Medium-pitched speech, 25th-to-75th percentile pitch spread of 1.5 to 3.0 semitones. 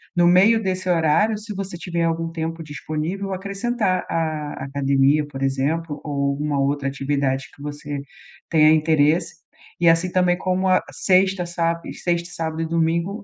No: medium, 165 Hz; average, 3.7 semitones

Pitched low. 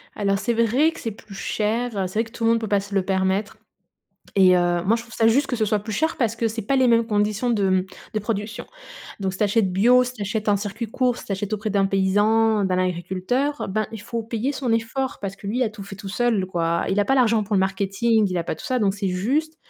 No: high, 215 Hz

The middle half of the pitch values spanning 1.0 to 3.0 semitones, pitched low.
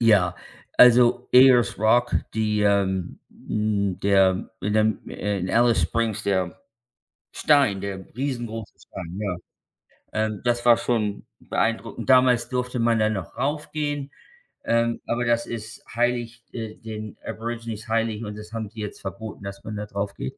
Yes: average, 2.7 semitones; low, 110 Hz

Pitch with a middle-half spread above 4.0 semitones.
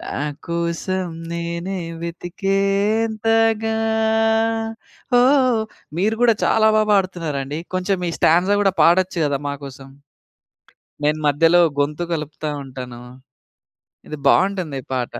Yes: average, 4.6 semitones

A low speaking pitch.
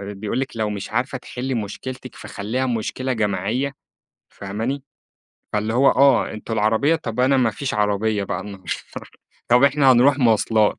Yes: low, 115 Hz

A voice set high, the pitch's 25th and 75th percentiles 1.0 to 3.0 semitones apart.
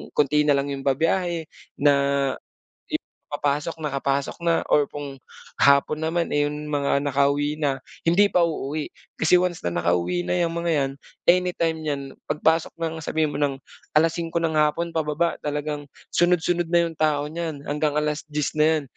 No: medium, 150 Hz; narrow, 2.4 semitones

